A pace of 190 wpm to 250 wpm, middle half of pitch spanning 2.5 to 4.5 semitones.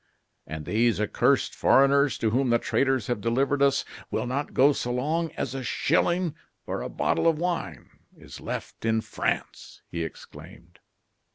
No: average, 160 wpm; average, 4.0 semitones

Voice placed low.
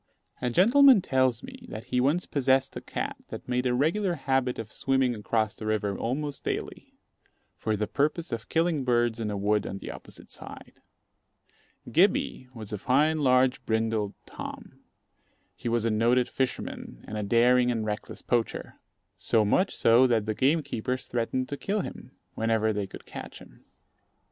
Yes: low, 125 Hz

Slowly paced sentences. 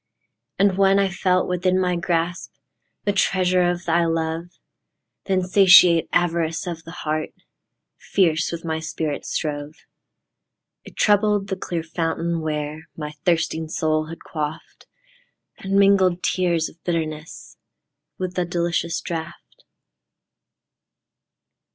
Yes: slow, 110 wpm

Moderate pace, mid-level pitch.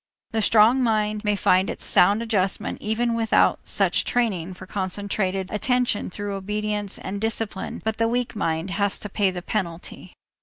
No: average, 160 wpm; high, 210 Hz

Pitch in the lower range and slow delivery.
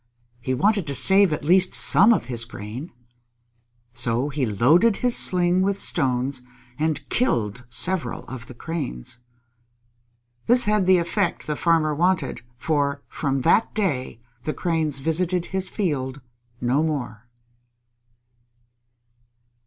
No: medium, 155 Hz; slow, 125 wpm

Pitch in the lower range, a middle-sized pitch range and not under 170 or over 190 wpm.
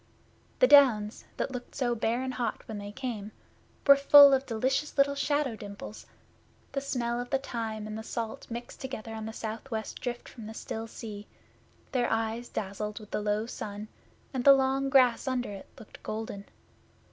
No: high, 235 Hz; average, 3.4 semitones; average, 180 wpm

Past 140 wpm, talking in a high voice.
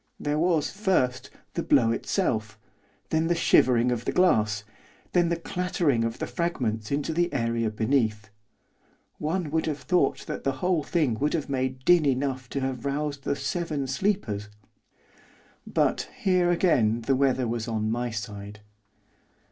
No: average, 150 wpm; low, 135 Hz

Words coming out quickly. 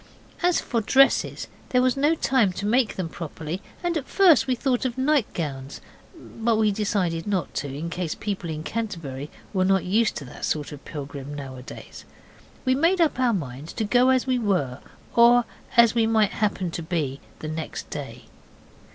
No: average, 175 wpm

